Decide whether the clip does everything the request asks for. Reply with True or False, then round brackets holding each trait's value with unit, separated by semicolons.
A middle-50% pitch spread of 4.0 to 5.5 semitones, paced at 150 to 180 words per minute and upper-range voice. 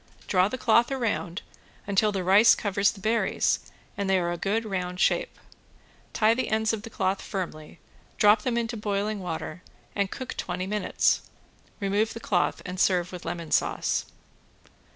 False (3.2 semitones; 165 wpm; 200 Hz)